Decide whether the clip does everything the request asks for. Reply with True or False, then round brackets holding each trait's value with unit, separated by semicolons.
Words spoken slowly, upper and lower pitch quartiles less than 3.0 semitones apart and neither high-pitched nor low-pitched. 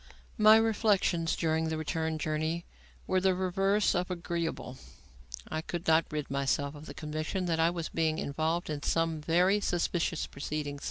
False (160 wpm; 2.5 semitones; 165 Hz)